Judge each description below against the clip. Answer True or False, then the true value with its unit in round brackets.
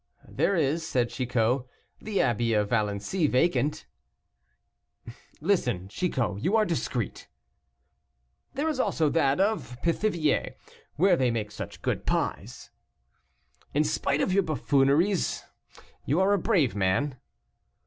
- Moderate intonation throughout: False (7.2 semitones)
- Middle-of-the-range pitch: True (145 Hz)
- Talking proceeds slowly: True (120 wpm)